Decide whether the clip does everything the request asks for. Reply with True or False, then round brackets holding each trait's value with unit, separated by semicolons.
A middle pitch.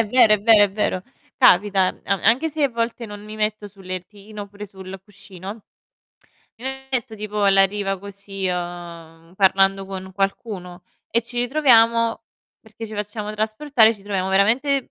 False (205 Hz)